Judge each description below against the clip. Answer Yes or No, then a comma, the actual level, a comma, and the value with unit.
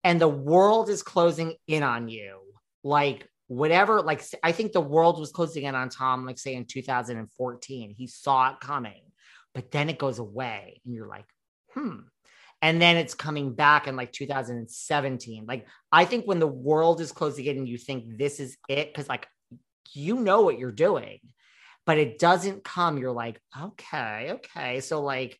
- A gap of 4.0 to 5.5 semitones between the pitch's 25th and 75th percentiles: Yes, average, 4.4 semitones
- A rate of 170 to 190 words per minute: Yes, average, 180 wpm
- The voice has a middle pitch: Yes, medium, 145 Hz